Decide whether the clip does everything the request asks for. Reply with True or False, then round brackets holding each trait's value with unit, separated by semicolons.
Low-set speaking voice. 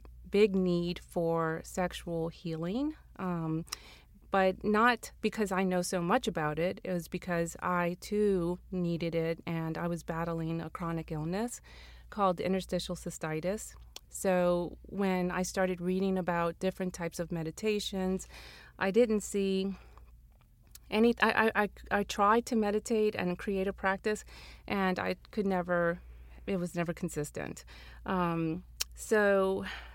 False (180 Hz)